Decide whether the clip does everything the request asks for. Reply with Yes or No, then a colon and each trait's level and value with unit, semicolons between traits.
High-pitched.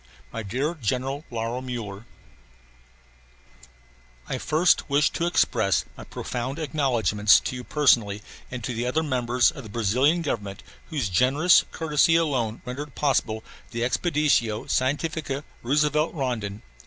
No: low, 130 Hz